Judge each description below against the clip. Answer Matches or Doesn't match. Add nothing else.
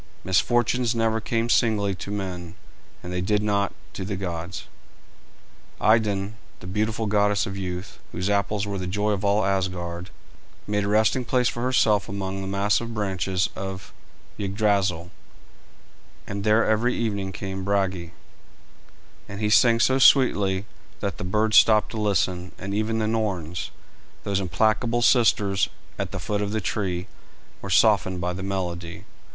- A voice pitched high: Doesn't match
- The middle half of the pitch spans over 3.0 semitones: Doesn't match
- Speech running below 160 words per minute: Matches